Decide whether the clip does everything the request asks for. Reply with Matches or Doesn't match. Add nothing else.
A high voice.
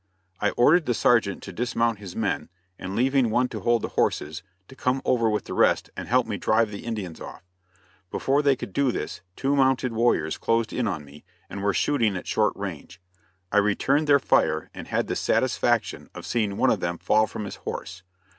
Doesn't match